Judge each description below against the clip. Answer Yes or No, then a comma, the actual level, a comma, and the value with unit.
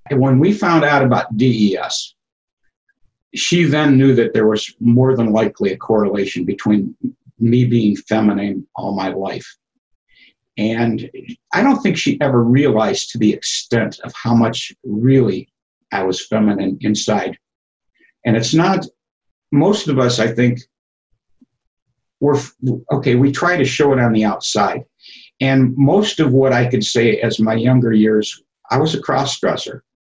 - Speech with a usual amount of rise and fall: Yes, average, 4.4 semitones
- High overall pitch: No, low, 125 Hz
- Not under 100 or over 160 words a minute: Yes, average, 155 wpm